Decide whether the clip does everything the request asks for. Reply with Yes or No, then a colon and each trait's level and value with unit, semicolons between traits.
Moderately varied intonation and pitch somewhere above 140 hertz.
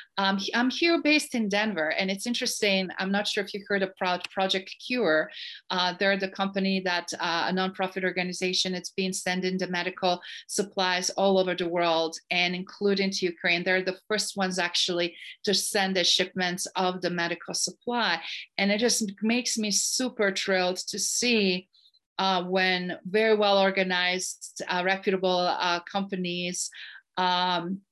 No: narrow, 1.9 semitones; high, 190 Hz